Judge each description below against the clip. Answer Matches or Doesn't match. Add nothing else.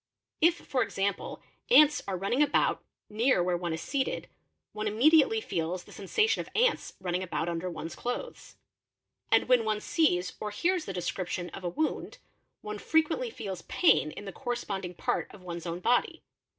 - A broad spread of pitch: Matches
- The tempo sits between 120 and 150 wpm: Doesn't match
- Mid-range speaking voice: Doesn't match